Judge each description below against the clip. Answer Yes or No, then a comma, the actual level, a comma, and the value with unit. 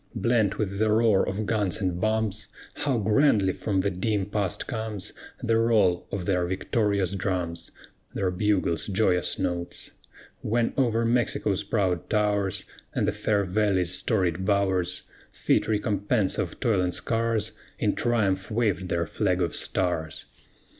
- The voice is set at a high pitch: No, low, 100 Hz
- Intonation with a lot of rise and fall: No, average, 3.0 semitones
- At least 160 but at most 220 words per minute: No, average, 140 wpm